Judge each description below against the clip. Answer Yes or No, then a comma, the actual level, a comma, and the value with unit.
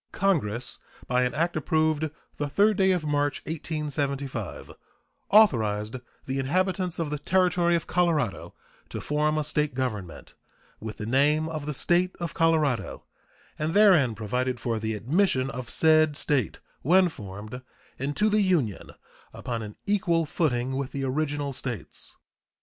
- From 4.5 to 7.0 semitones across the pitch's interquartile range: Yes, average, 5.0 semitones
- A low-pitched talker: No, medium, 145 Hz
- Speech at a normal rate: Yes, average, 145 wpm